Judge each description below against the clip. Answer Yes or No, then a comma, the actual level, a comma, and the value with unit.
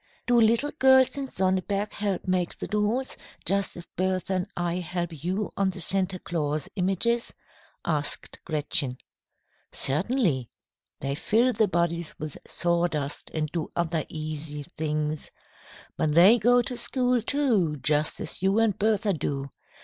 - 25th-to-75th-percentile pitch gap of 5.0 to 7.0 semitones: Yes, wide, 5.4 semitones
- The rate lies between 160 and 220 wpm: No, average, 140 wpm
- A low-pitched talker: No, medium, 185 Hz